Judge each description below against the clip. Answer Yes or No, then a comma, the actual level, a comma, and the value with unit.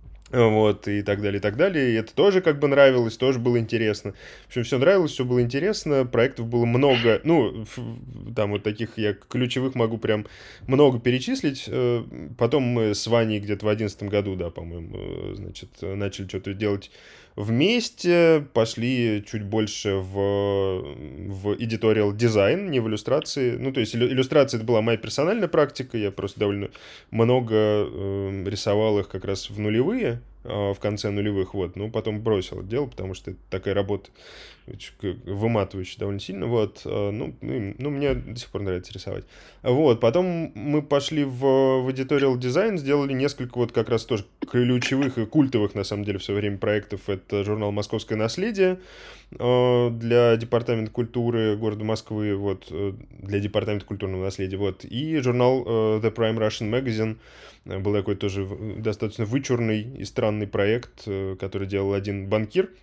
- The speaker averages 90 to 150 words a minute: No, fast, 160 wpm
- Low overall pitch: Yes, low, 110 Hz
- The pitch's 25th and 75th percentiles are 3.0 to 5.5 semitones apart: Yes, average, 3.6 semitones